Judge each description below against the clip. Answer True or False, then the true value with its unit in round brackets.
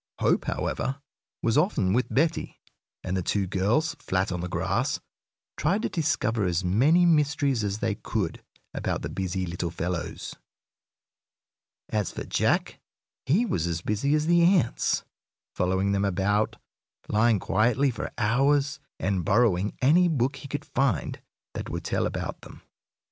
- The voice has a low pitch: True (110 Hz)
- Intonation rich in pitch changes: True (7.2 semitones)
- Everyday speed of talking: True (150 wpm)